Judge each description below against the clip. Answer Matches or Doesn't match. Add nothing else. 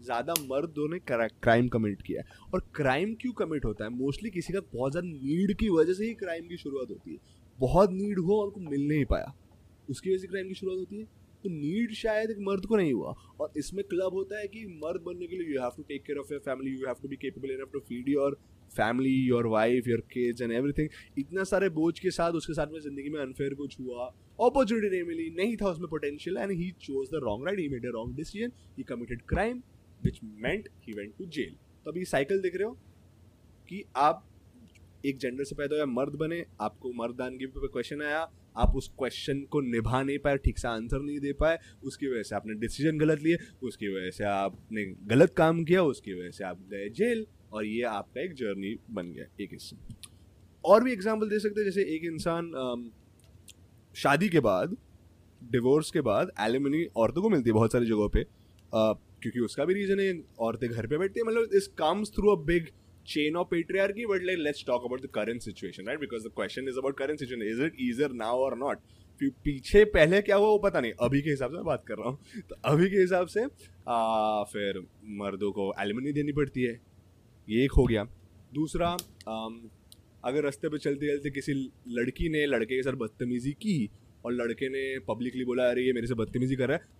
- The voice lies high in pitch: Doesn't match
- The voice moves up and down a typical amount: Doesn't match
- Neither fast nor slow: Doesn't match